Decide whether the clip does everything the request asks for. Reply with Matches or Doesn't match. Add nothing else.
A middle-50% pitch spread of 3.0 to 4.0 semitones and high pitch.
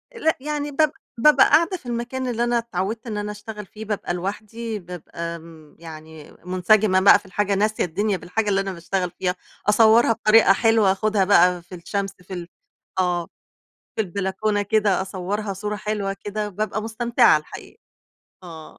Matches